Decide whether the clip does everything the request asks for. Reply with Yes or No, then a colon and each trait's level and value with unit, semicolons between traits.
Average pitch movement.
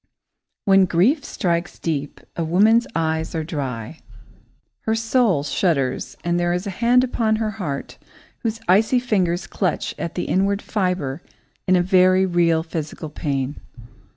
Yes: average, 4.8 semitones